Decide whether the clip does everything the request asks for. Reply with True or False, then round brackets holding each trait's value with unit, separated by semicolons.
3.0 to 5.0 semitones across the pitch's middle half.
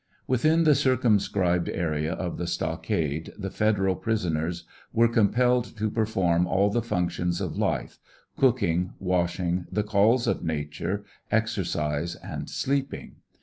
True (4.7 semitones)